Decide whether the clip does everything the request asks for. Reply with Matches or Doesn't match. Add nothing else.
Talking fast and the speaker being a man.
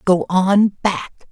Doesn't match